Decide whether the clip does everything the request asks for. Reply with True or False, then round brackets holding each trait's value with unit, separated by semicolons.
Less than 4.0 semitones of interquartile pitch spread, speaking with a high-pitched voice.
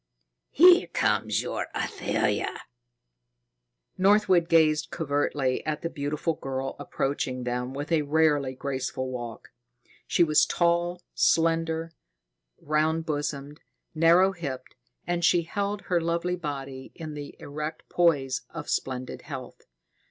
False (3.6 semitones; 155 Hz)